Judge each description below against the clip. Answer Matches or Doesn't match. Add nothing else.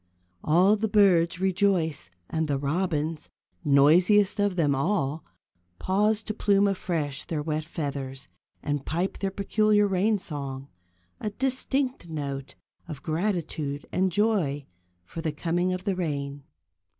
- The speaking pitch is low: Doesn't match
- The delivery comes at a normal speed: Doesn't match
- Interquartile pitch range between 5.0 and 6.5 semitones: Matches